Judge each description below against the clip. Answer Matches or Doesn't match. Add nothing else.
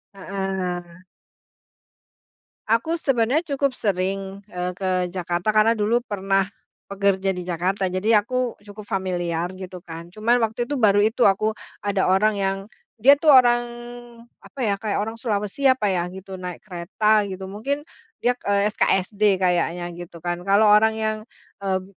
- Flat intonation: Doesn't match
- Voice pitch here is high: Matches